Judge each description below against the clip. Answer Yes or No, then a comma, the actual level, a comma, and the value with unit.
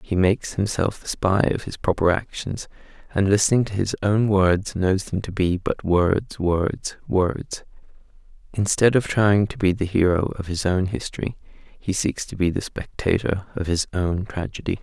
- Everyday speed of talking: Yes, average, 180 wpm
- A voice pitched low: Yes, very low, 95 Hz